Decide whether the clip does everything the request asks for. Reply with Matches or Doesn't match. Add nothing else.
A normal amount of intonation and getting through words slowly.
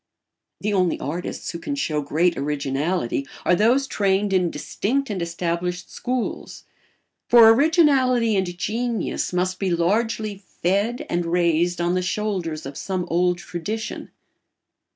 Matches